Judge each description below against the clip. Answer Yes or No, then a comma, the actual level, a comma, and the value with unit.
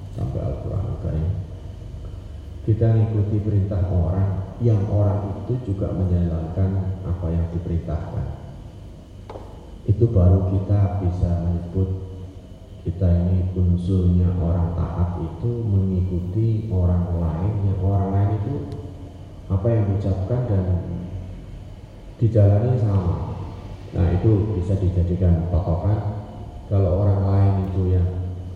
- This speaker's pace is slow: No, average, 105 wpm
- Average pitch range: No, narrow, 2.2 semitones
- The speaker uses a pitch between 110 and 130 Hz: No, very low, 95 Hz